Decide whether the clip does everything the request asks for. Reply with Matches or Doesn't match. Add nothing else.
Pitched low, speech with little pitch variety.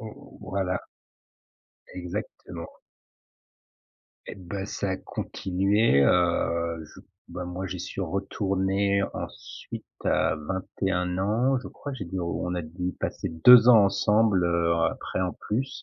Matches